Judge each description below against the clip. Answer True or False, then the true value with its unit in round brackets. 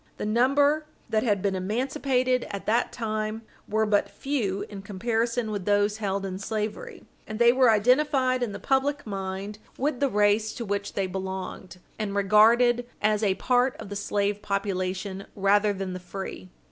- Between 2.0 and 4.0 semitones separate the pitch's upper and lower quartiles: True (3.5 semitones)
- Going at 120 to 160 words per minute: False (170 wpm)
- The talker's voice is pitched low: False (210 Hz)